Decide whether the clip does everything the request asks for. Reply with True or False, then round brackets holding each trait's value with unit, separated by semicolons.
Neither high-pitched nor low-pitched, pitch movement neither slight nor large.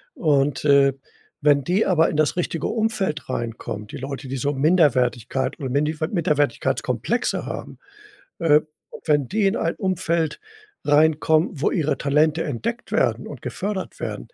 True (150 Hz; 3.5 semitones)